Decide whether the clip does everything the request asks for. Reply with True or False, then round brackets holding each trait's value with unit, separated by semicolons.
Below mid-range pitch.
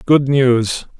True (130 Hz)